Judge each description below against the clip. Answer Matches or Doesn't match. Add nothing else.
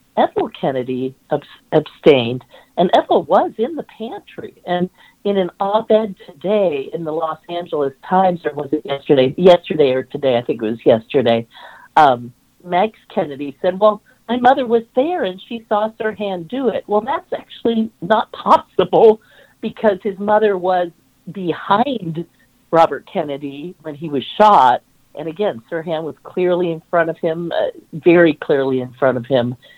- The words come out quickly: Doesn't match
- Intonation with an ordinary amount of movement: Doesn't match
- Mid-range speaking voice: Matches